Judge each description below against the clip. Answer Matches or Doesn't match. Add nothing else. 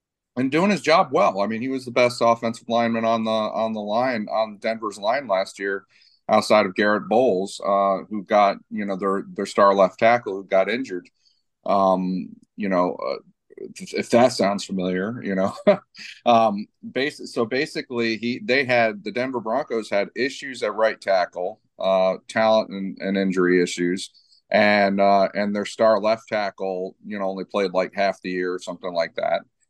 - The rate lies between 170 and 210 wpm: Matches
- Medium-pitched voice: Doesn't match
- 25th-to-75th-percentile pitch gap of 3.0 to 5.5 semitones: Matches